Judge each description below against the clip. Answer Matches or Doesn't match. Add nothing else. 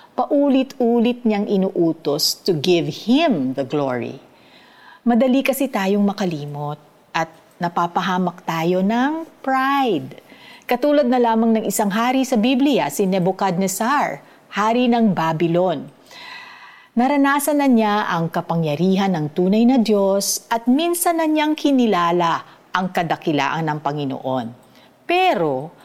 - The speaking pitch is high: Matches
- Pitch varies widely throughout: Matches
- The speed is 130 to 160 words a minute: Doesn't match